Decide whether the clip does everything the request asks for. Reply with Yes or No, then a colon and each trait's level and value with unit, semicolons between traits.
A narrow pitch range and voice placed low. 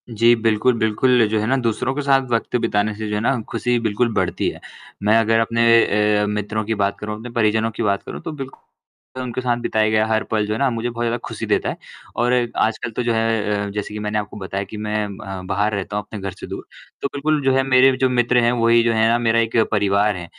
Yes: narrow, 2.3 semitones; low, 110 Hz